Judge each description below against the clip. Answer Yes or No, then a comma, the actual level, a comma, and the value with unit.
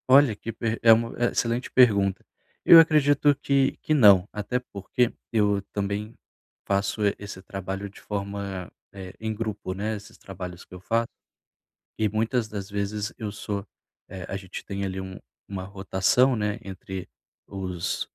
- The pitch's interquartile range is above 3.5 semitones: No, average, 2.9 semitones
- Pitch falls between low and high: No, low, 100 Hz